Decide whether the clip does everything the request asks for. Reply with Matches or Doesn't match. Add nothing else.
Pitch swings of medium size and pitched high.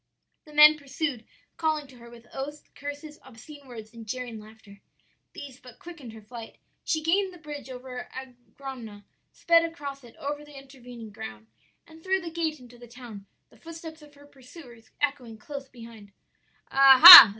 Matches